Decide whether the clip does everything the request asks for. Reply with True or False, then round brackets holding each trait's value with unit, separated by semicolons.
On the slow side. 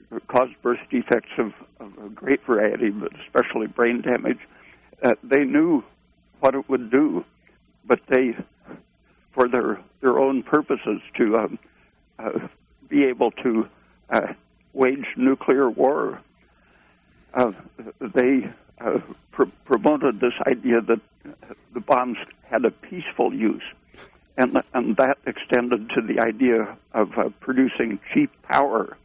True (130 wpm)